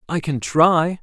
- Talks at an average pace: Yes, average, 175 wpm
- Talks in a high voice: No, medium, 160 Hz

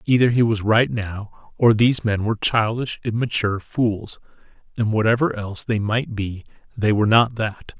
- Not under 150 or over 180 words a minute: Yes, average, 160 wpm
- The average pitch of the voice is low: Yes, low, 110 Hz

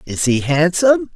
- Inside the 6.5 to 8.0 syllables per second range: No, 5.0 syllables/s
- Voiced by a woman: No, male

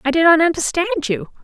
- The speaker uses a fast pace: Yes, fast, 210 wpm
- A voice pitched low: No, very high, 300 Hz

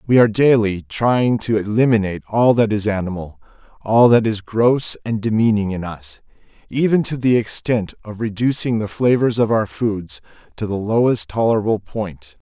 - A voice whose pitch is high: No, low, 110 Hz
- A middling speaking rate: Yes, average, 165 wpm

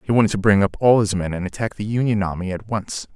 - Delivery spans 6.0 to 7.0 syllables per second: Yes, 6.4 syllables/s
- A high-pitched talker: No, low, 100 Hz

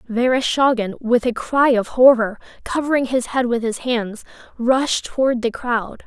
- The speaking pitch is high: Yes, high, 245 Hz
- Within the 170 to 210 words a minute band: No, average, 160 wpm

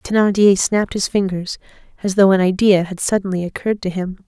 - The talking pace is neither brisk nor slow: Yes, average, 185 wpm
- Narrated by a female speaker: Yes, female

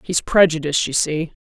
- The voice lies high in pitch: No, medium, 160 Hz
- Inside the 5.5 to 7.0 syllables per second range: Yes, 5.6 syllables/s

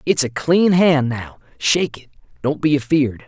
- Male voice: Yes, male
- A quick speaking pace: No, average, 185 wpm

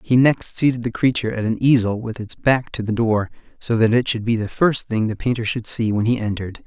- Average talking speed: No, fast, 260 wpm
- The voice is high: No, low, 115 Hz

